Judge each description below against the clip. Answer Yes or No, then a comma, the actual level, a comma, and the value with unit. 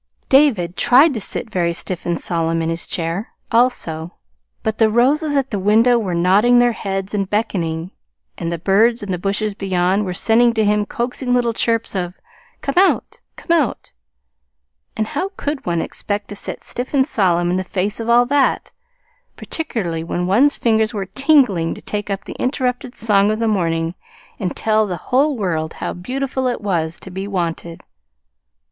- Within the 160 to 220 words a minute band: Yes, average, 180 wpm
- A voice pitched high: Yes, high, 210 Hz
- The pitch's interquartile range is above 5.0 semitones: Yes, wide, 5.4 semitones